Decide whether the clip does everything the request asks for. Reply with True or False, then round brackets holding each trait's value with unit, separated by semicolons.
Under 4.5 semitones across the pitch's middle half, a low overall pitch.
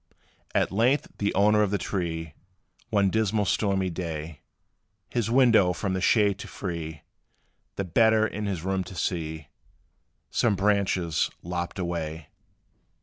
True (3.8 semitones; 95 Hz)